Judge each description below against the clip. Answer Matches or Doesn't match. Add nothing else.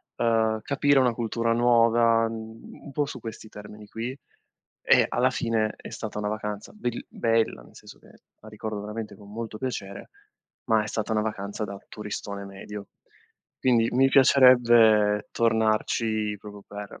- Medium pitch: Doesn't match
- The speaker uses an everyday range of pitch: Doesn't match